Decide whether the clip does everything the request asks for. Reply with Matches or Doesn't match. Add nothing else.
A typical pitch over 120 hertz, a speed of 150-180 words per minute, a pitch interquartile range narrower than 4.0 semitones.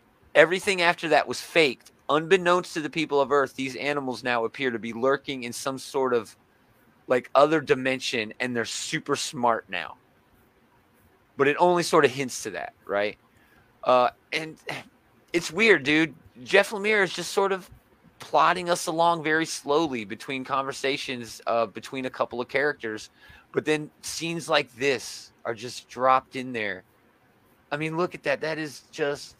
Doesn't match